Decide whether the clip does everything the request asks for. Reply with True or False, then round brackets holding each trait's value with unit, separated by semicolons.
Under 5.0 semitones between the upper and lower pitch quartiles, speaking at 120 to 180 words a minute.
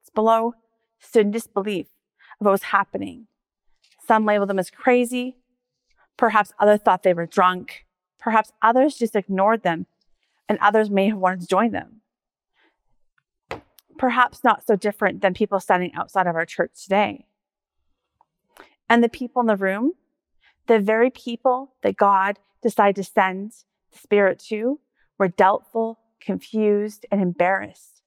True (3.3 semitones; 140 wpm)